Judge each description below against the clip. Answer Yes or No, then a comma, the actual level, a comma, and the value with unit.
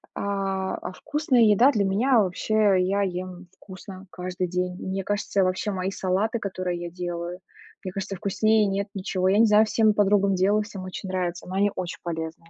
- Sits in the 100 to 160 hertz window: No, high, 190 Hz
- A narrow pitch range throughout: Yes, narrow, 2.1 semitones